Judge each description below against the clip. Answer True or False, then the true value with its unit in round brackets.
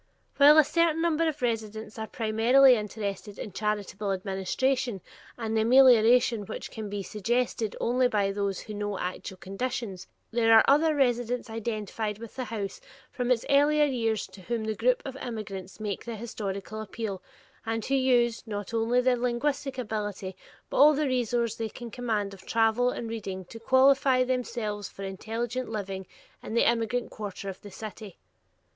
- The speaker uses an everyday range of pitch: True (3.3 semitones)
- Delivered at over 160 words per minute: True (170 wpm)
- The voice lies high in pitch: True (225 Hz)